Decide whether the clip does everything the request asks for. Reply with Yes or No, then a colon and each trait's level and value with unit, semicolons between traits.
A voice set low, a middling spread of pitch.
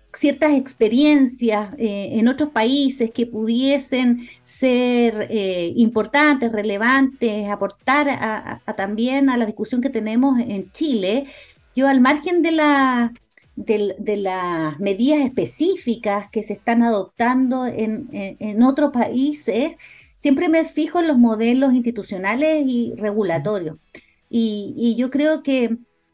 No: high, 240 Hz; average, 4.2 semitones